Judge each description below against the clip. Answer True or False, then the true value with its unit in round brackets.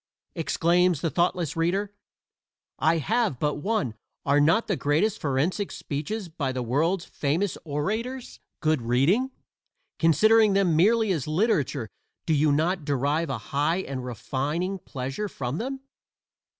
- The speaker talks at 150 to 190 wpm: False (135 wpm)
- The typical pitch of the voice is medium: True (165 Hz)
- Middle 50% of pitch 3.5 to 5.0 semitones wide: False (5.6 semitones)